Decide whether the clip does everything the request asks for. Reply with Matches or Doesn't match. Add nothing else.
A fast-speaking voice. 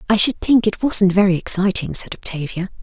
Doesn't match